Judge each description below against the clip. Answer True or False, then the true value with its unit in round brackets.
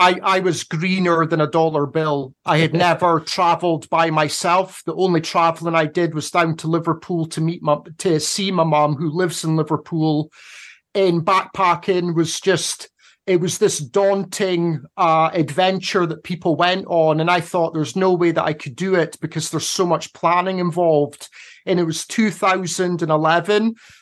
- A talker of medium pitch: True (170 Hz)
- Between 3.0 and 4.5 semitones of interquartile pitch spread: False (2.4 semitones)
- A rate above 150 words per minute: True (170 wpm)